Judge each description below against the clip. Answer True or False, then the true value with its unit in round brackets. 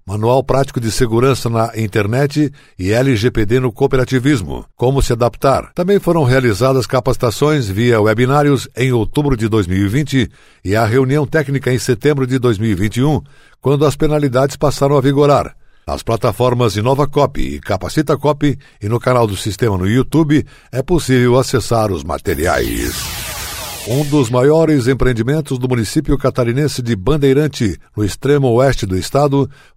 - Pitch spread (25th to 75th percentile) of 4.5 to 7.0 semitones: False (3.7 semitones)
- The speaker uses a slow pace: False (140 wpm)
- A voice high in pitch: False (130 Hz)